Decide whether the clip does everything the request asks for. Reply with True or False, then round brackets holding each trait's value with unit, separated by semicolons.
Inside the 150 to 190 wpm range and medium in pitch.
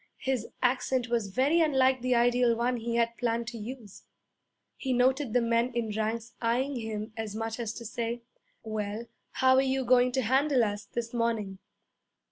False (175 wpm; 235 Hz)